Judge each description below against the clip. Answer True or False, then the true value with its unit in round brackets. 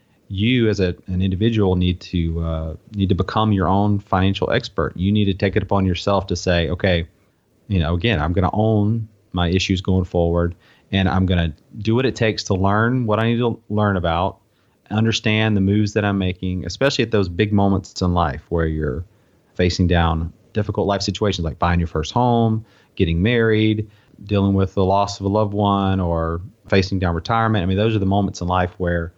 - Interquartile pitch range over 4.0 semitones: False (3.1 semitones)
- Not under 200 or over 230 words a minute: True (205 wpm)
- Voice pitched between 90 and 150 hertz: True (95 Hz)